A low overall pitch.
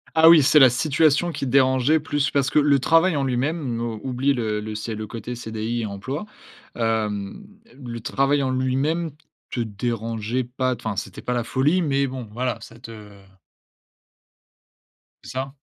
Yes: low, 130 Hz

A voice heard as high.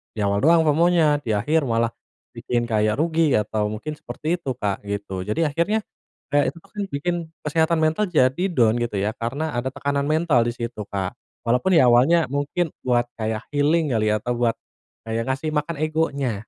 No: low, 130 Hz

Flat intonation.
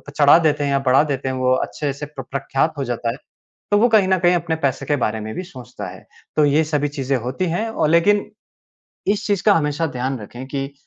No: average, 4.6 semitones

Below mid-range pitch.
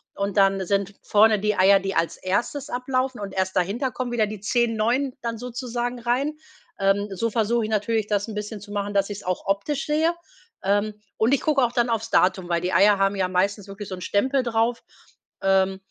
No: high, 210 Hz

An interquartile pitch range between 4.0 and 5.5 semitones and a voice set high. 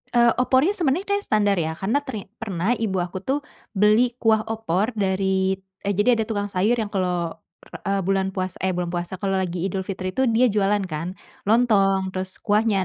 No: average, 2.9 semitones; high, 200 Hz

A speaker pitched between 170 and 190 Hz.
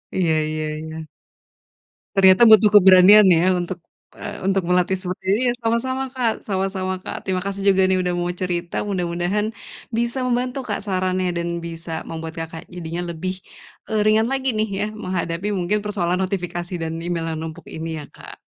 Yes: medium, 185 Hz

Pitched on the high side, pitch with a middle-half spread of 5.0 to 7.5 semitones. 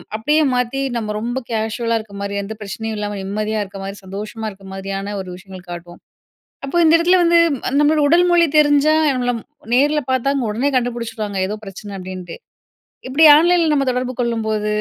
Yes: high, 225 Hz; wide, 5.4 semitones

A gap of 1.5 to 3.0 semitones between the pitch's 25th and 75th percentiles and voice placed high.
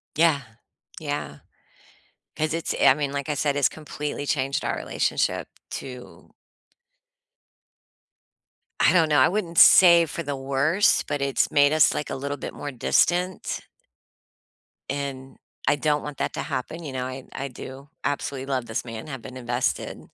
No: narrow, 2.5 semitones; medium, 140 Hz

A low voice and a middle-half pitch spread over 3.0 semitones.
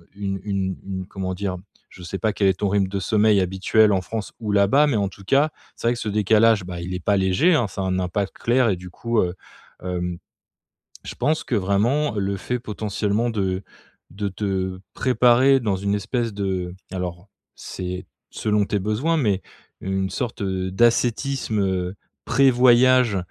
Yes: low, 100 Hz; average, 3.6 semitones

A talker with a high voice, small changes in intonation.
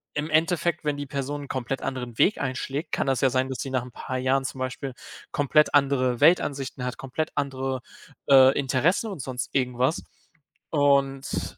No: low, 135 Hz; narrow, 1.9 semitones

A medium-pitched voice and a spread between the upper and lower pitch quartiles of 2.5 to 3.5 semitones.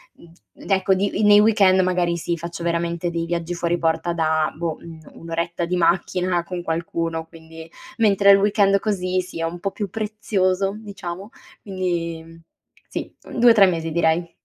Yes: medium, 175 Hz; average, 2.8 semitones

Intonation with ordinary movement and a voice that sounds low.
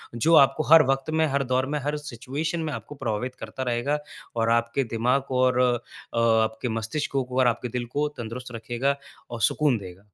Yes: average, 3.2 semitones; low, 125 Hz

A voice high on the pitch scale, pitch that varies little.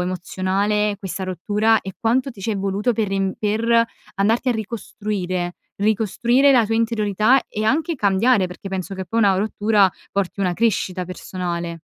No: high, 205 Hz; average, 3.1 semitones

